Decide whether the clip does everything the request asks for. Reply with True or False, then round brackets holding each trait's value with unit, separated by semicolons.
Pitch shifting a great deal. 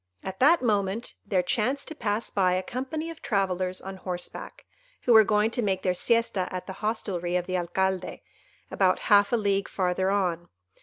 False (3.3 semitones)